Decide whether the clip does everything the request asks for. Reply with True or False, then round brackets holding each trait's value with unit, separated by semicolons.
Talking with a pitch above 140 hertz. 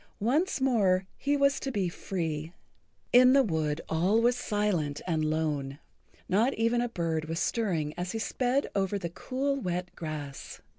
True (190 Hz)